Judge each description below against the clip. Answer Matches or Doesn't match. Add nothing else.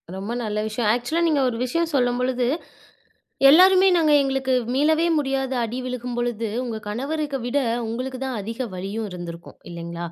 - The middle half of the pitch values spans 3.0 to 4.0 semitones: Matches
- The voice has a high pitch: Matches